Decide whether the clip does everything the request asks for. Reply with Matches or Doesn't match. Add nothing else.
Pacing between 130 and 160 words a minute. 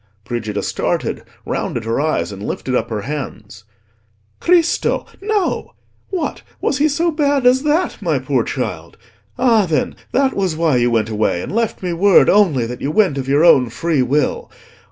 Doesn't match